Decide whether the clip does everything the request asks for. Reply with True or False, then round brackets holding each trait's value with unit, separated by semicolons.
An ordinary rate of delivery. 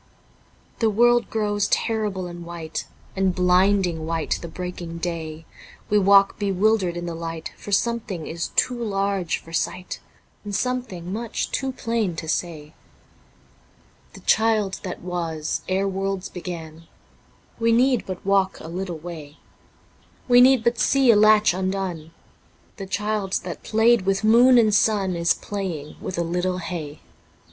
True (150 wpm)